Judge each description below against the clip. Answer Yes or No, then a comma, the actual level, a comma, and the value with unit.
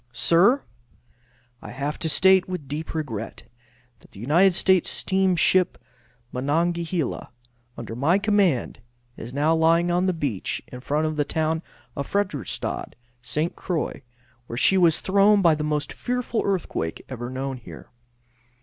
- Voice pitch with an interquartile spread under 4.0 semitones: No, average, 5.0 semitones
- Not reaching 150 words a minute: Yes, average, 140 wpm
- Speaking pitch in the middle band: Yes, medium, 160 Hz